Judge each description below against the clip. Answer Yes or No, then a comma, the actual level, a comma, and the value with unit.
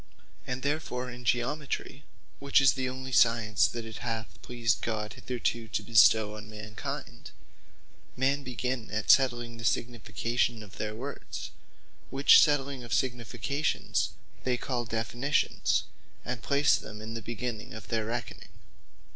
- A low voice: Yes, low, 120 Hz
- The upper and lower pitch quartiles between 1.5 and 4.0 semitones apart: Yes, average, 2.8 semitones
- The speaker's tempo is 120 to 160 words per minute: Yes, average, 140 wpm